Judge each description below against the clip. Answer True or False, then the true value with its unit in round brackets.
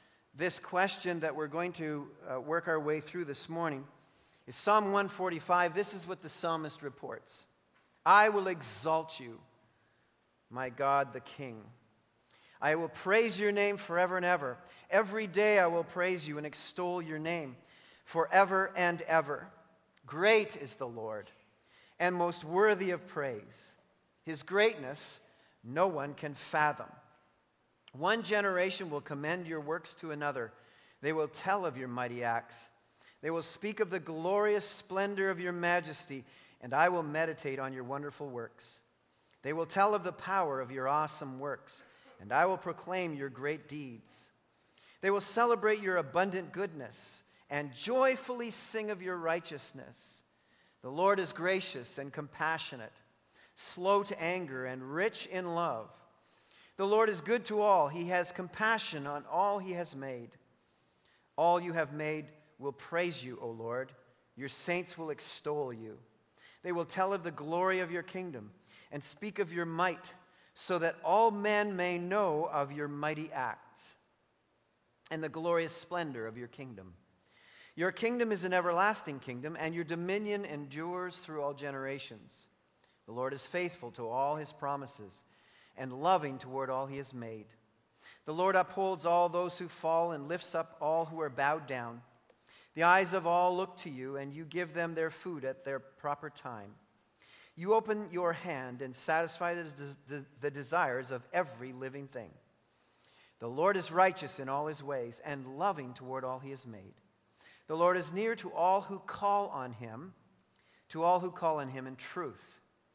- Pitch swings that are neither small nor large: True (4.9 semitones)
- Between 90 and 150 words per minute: False (160 wpm)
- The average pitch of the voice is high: False (165 Hz)